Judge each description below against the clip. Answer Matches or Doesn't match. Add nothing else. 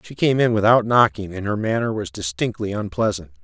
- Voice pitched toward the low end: Matches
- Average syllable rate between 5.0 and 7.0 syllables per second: Matches